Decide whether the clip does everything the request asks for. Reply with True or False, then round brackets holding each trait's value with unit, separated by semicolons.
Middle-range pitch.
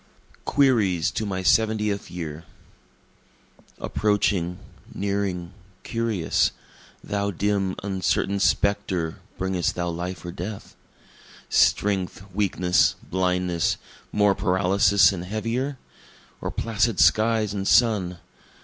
False (100 Hz)